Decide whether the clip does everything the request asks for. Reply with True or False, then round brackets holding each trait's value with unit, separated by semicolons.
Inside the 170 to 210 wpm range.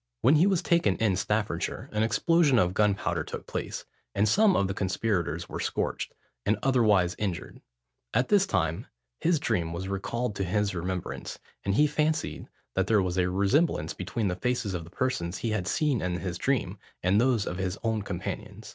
True (180 wpm)